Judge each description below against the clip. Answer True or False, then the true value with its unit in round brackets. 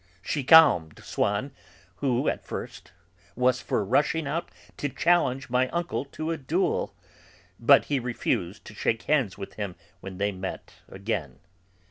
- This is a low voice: True (125 Hz)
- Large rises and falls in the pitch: True (6.5 semitones)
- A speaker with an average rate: True (145 wpm)